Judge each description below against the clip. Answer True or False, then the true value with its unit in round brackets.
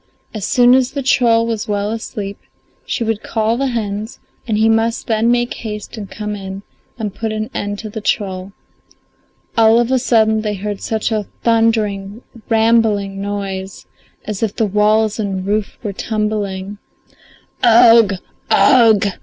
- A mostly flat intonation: True (2.0 semitones)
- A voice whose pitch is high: True (215 Hz)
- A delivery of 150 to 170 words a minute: True (160 wpm)